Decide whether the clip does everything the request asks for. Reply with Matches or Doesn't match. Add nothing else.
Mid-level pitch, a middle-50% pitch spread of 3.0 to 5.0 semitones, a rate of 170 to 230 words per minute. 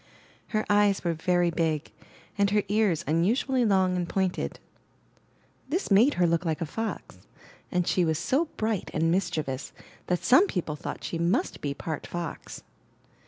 Doesn't match